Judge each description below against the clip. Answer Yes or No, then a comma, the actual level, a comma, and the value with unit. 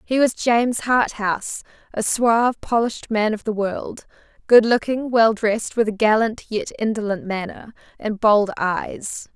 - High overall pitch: Yes, high, 220 Hz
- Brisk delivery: No, average, 155 wpm